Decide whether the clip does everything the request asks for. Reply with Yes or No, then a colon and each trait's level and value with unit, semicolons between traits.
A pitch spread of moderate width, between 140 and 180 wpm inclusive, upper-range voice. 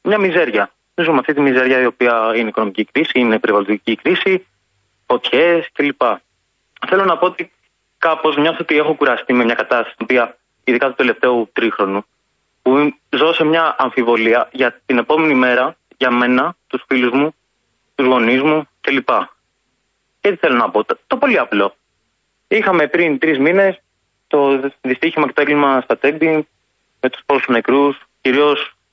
No: average, 3.9 semitones; fast, 170 wpm; low, 135 Hz